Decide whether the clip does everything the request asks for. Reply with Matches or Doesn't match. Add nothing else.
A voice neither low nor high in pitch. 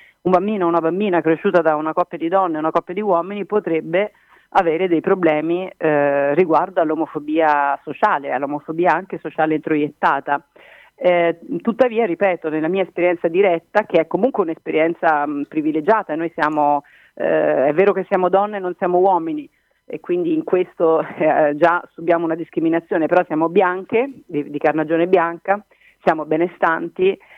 Matches